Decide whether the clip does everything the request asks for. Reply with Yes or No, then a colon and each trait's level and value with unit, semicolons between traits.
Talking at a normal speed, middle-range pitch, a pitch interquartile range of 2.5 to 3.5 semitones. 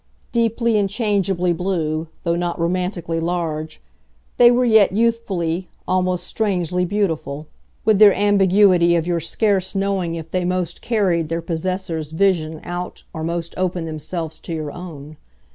Yes: average, 145 wpm; medium, 180 Hz; average, 3.1 semitones